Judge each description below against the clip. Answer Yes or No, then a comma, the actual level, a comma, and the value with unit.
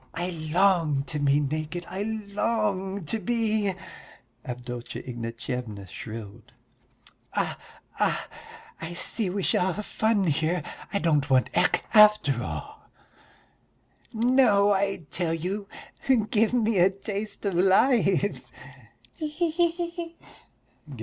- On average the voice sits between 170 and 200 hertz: Yes, high, 190 Hz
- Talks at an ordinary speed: No, slow, 115 wpm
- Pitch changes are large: Yes, wide, 6.3 semitones